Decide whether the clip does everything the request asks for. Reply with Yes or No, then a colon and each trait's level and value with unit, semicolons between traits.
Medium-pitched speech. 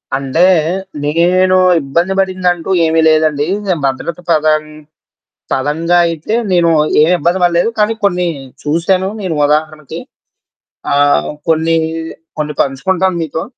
Yes: medium, 165 Hz